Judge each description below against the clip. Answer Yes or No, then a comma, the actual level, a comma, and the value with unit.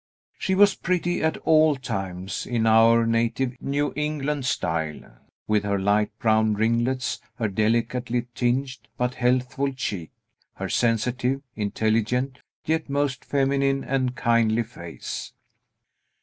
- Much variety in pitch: No, average, 3.8 semitones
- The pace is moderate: No, slow, 120 wpm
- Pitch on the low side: Yes, low, 125 Hz